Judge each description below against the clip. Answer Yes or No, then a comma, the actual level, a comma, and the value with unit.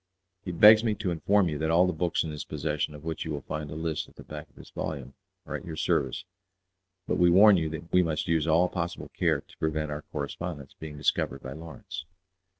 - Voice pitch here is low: Yes, very low, 80 Hz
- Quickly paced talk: Yes, fast, 235 wpm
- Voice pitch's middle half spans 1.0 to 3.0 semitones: Yes, average, 2.7 semitones